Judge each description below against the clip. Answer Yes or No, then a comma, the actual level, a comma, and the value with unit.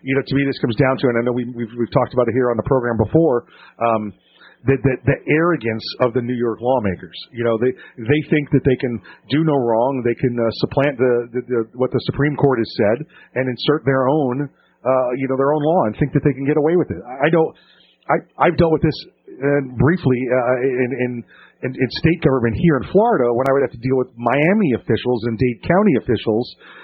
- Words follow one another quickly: Yes, fast, 230 wpm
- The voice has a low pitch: Yes, low, 130 Hz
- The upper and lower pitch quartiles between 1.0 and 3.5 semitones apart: Yes, average, 3.1 semitones